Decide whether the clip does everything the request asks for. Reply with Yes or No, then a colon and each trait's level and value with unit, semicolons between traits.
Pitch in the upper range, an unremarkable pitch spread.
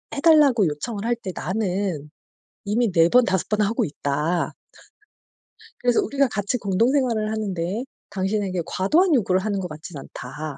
Yes: high, 200 Hz; average, 4.8 semitones